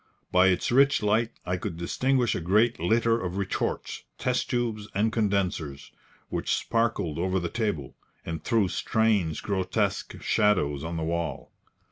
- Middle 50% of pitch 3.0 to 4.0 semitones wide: No, average, 4.8 semitones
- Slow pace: No, average, 145 wpm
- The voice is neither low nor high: No, low, 100 Hz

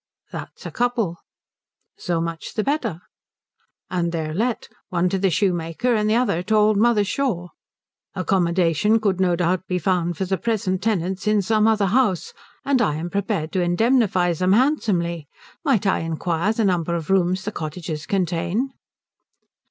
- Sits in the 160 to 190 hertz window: Yes, medium, 185 Hz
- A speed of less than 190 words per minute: Yes, average, 160 wpm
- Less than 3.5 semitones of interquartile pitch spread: No, average, 3.9 semitones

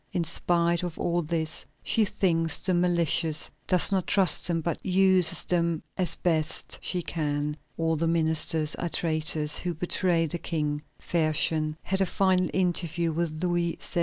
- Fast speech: No, average, 160 wpm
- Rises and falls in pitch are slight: Yes, narrow, 2.0 semitones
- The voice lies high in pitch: No, medium, 170 Hz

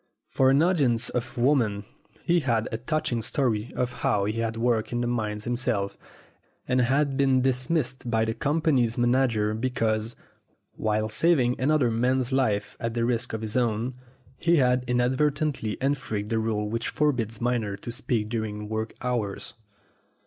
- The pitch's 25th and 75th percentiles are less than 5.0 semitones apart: Yes, average, 2.9 semitones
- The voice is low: Yes, low, 120 Hz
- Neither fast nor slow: Yes, average, 155 wpm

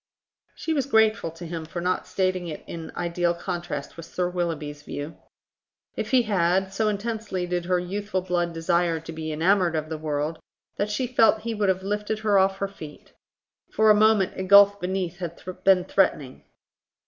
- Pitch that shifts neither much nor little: Yes, average, 3.4 semitones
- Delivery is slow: No, average, 185 wpm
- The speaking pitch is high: No, medium, 180 Hz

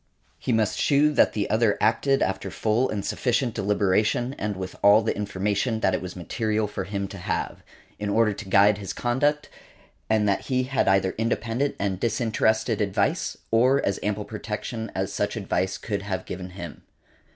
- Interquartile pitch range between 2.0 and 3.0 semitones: Yes, narrow, 2.6 semitones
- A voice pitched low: Yes, low, 105 Hz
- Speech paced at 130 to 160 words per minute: No, average, 175 wpm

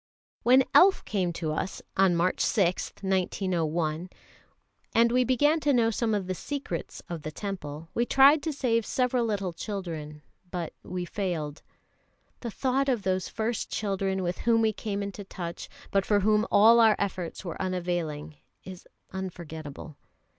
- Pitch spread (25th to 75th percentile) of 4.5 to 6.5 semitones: Yes, average, 4.8 semitones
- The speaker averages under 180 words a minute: Yes, average, 160 wpm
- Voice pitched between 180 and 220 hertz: Yes, high, 190 Hz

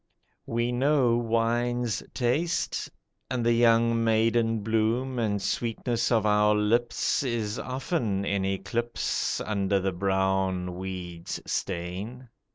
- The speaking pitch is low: Yes, low, 115 Hz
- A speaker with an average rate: No, slow, 110 wpm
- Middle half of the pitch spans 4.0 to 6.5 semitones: No, average, 3.5 semitones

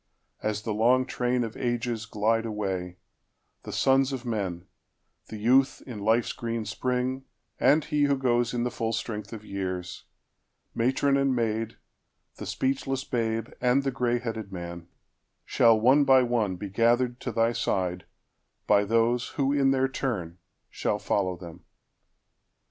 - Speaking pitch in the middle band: No, low, 115 Hz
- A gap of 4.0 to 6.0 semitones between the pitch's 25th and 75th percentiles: No, average, 3.5 semitones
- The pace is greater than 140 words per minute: No, slow, 135 wpm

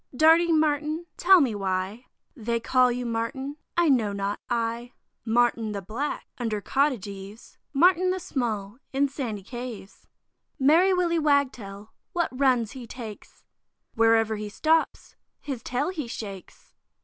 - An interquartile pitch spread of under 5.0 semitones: No, average, 5.3 semitones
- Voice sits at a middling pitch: No, high, 245 Hz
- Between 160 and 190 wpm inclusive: No, slow, 135 wpm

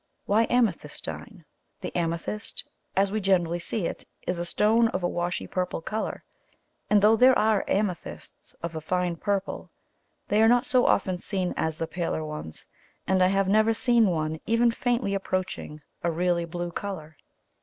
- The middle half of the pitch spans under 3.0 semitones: No, average, 4.0 semitones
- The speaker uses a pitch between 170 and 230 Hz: Yes, high, 190 Hz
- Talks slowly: No, average, 165 wpm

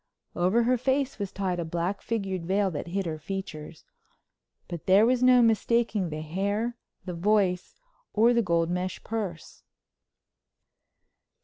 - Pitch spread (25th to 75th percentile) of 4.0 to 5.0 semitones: Yes, average, 4.6 semitones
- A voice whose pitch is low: No, high, 195 Hz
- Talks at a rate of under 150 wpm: Yes, average, 140 wpm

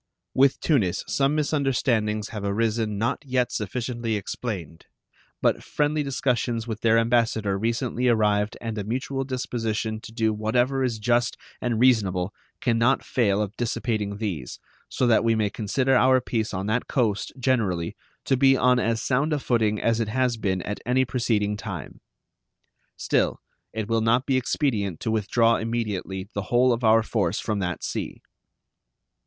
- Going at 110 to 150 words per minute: No, average, 160 wpm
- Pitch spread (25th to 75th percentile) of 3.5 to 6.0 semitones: No, average, 3.0 semitones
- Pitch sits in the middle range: No, low, 115 Hz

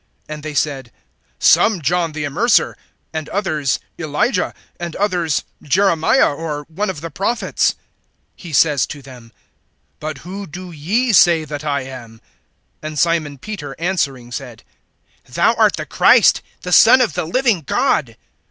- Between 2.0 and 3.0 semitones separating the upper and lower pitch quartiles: No, average, 4.3 semitones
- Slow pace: No, average, 145 wpm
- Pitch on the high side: No, medium, 160 Hz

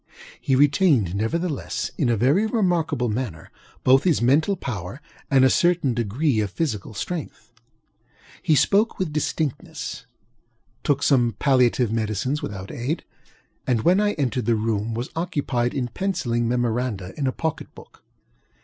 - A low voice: Yes, low, 130 Hz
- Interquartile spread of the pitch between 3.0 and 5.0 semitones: No, wide, 5.4 semitones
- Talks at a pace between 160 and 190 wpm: No, slow, 135 wpm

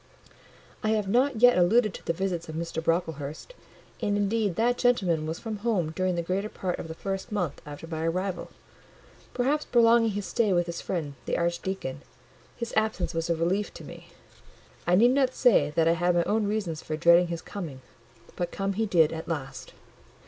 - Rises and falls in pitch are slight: No, average, 4.6 semitones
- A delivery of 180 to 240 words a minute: Yes, average, 190 wpm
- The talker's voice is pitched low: No, medium, 180 Hz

